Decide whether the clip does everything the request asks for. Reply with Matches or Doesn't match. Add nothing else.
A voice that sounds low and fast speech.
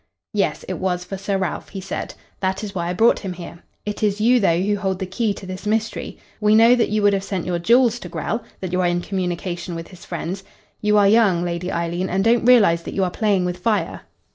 Doesn't match